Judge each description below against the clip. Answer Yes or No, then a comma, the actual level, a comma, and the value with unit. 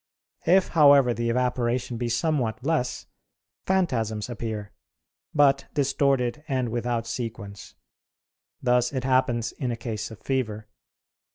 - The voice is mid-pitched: No, low, 125 Hz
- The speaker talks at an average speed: No, slow, 115 wpm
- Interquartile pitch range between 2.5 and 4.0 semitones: Yes, average, 3.0 semitones